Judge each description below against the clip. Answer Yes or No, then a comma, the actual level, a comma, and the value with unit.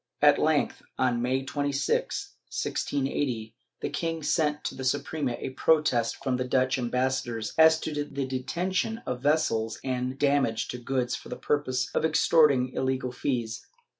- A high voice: No, low, 130 Hz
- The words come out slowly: No, average, 150 wpm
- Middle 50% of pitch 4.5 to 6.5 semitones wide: No, average, 2.9 semitones